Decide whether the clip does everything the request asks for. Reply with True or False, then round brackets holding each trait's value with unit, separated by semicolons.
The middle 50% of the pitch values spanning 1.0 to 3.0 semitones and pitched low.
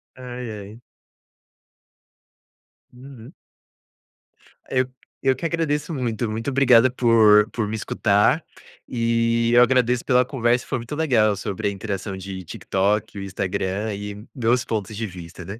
False (3.5 semitones; 115 Hz)